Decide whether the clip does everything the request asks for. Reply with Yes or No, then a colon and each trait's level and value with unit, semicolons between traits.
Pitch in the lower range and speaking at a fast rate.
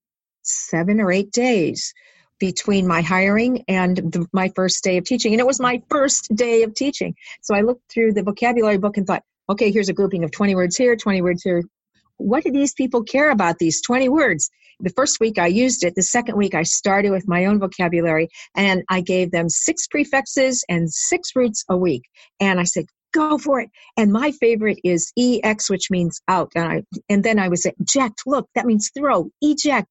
No: high, 210 Hz; fast, 210 wpm